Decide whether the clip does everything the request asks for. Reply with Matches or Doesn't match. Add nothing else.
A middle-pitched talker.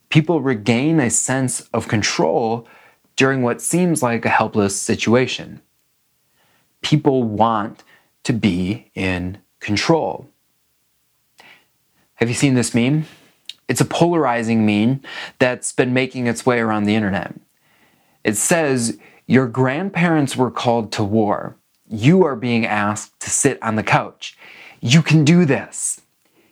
Doesn't match